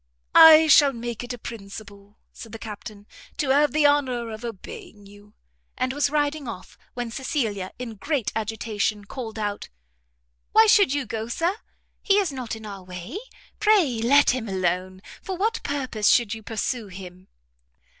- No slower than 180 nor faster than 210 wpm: No, average, 165 wpm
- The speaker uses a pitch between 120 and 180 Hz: No, high, 235 Hz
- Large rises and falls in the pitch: Yes, wide, 5.7 semitones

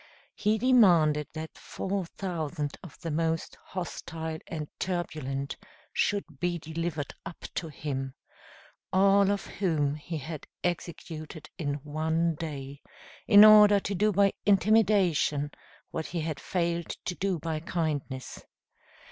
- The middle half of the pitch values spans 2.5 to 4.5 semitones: Yes, average, 3.8 semitones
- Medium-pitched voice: Yes, medium, 165 Hz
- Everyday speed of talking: No, slow, 125 wpm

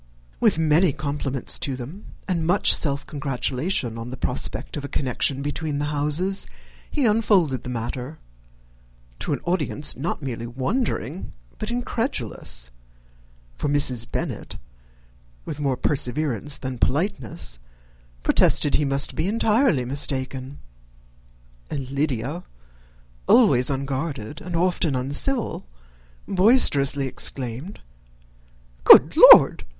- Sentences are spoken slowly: Yes, slow, 110 wpm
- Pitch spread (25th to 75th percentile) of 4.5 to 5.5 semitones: Yes, average, 5.0 semitones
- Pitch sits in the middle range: Yes, medium, 145 Hz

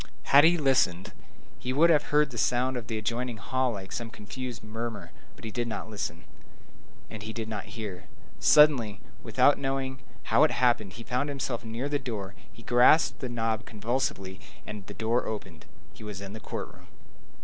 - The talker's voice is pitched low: Yes, low, 115 Hz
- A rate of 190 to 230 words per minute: Yes, average, 195 wpm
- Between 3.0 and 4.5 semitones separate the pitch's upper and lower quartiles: Yes, average, 3.3 semitones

